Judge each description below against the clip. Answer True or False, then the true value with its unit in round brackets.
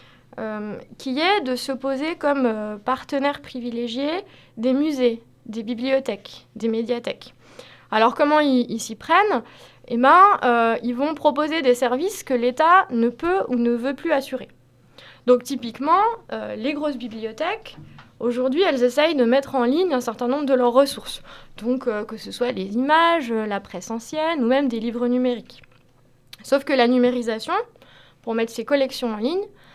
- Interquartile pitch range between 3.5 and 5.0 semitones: True (4.0 semitones)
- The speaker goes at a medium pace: True (165 wpm)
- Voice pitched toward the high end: True (250 Hz)